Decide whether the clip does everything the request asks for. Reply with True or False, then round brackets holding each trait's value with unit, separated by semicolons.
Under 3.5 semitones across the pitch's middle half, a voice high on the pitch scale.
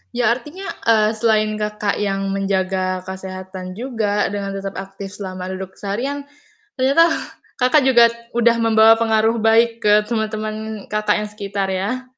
True (2.9 semitones; 215 Hz)